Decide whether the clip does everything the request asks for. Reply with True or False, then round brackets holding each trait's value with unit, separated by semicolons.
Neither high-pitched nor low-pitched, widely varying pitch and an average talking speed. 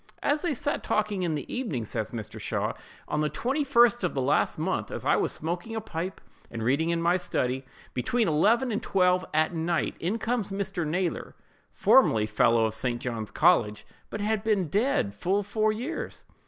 True (180 Hz; 7.6 semitones; 185 wpm)